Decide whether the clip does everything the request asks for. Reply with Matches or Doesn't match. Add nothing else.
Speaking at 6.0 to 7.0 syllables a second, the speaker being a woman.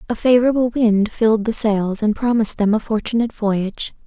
Doesn't match